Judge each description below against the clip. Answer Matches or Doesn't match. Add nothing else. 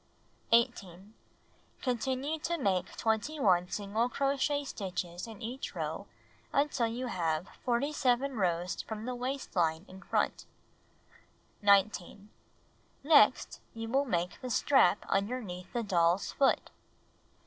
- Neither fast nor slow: Doesn't match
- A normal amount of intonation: Doesn't match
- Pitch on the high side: Matches